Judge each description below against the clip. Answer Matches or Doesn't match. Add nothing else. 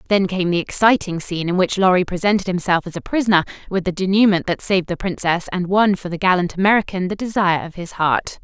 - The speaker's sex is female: Matches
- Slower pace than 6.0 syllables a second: Doesn't match